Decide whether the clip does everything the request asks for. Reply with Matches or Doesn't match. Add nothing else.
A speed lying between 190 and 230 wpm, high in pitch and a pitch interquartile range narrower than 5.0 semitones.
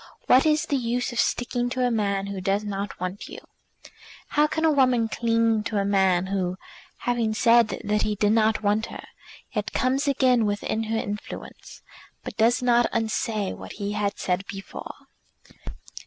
Doesn't match